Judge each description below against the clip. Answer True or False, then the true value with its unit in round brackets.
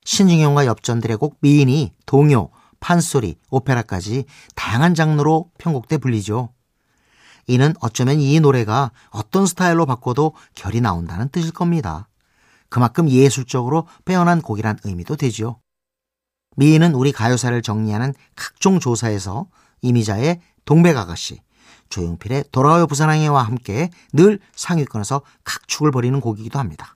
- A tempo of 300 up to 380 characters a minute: True (320 characters per minute)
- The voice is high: False (135 Hz)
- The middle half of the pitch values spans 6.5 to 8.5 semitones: False (5.2 semitones)